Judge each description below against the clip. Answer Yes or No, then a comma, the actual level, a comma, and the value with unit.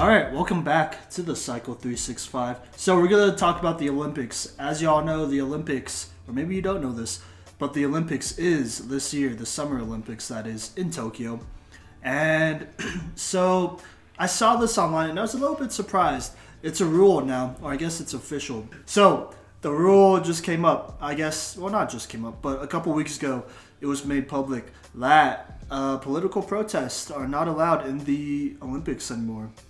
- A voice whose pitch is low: No, medium, 145 Hz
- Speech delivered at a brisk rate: No, average, 190 wpm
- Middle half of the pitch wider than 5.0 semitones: Yes, wide, 5.5 semitones